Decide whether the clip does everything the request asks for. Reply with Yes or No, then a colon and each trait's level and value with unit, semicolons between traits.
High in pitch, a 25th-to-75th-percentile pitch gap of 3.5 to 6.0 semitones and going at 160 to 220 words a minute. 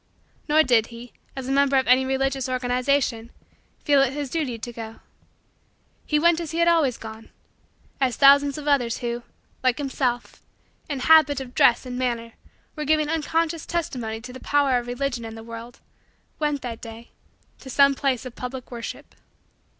No: very high, 260 Hz; average, 3.1 semitones; average, 175 wpm